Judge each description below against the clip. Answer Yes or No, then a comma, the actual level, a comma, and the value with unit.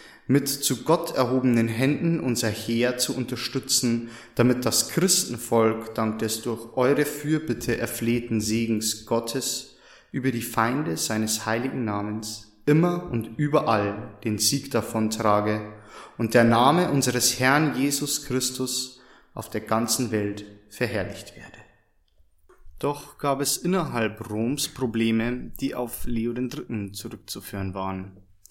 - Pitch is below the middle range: Yes, low, 120 Hz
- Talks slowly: Yes, slow, 120 wpm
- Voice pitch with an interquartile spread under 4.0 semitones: Yes, average, 3.1 semitones